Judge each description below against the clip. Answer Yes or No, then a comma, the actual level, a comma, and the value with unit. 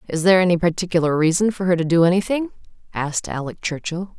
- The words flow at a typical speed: Yes, average, 185 wpm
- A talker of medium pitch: Yes, medium, 175 Hz